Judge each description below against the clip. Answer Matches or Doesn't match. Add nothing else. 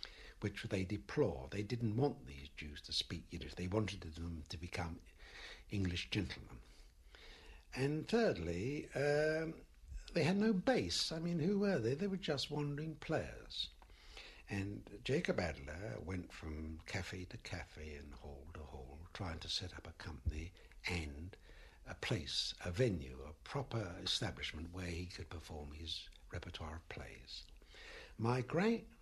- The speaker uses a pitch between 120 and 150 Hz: Doesn't match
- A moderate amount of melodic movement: Doesn't match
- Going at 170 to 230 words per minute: Doesn't match